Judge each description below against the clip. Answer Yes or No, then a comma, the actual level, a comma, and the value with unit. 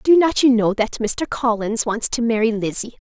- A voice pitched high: Yes, high, 230 Hz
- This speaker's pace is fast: Yes, fast, 215 wpm